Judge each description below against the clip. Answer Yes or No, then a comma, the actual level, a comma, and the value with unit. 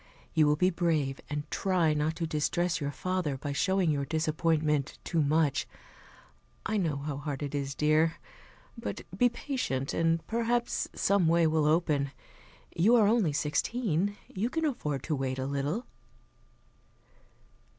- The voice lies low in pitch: No, medium, 160 Hz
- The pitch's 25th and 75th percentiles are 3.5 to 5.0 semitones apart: Yes, average, 4.2 semitones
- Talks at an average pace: Yes, average, 150 wpm